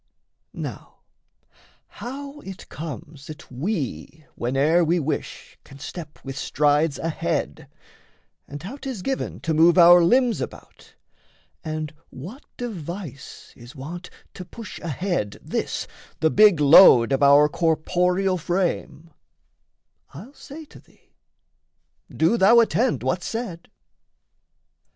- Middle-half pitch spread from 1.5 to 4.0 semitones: No, average, 4.8 semitones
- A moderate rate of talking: No, slow, 115 wpm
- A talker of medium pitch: Yes, medium, 170 Hz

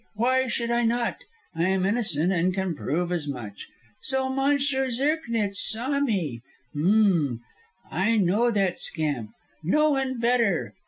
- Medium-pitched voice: No, high, 215 Hz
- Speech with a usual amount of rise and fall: No, wide, 6.6 semitones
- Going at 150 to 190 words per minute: No, average, 140 wpm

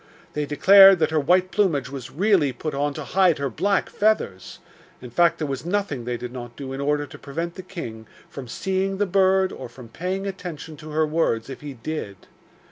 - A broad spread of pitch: Yes, wide, 5.8 semitones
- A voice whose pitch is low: No, medium, 155 Hz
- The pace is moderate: No, fast, 210 wpm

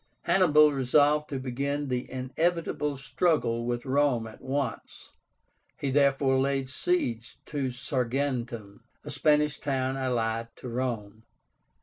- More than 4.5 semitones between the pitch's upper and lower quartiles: No, average, 2.9 semitones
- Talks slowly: Yes, slow, 115 wpm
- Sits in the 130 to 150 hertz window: Yes, low, 135 Hz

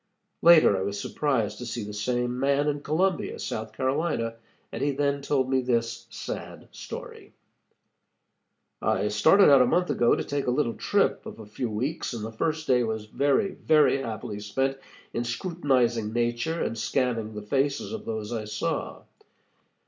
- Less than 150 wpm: No, average, 170 wpm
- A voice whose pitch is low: Yes, low, 125 Hz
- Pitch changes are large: No, average, 4.2 semitones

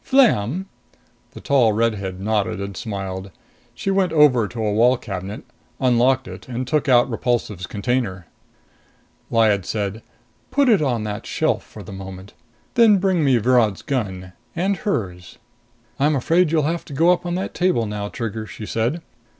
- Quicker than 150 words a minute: Yes, average, 165 wpm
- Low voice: Yes, low, 120 Hz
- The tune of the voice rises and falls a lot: Yes, wide, 6.9 semitones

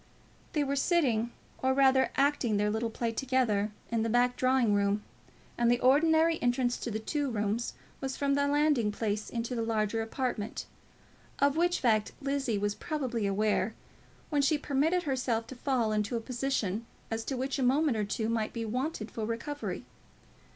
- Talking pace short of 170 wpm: No, average, 175 wpm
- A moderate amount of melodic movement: Yes, average, 3.9 semitones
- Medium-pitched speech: No, high, 245 Hz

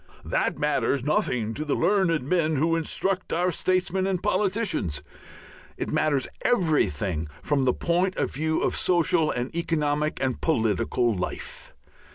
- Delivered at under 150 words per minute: Yes, average, 140 wpm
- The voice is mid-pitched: Yes, medium, 155 Hz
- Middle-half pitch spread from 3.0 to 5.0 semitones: No, wide, 5.5 semitones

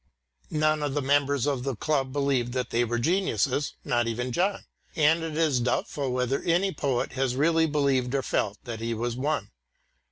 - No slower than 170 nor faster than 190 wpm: Yes, average, 185 wpm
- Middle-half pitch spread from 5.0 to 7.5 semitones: No, average, 3.6 semitones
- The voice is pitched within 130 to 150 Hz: Yes, low, 135 Hz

